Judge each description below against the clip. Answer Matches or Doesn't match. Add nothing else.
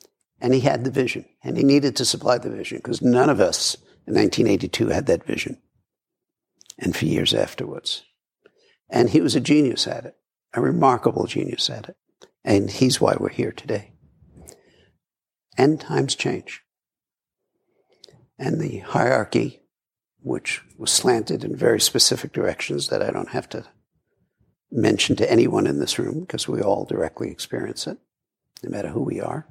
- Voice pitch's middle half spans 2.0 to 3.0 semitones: Matches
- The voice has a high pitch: Doesn't match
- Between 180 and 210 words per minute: Doesn't match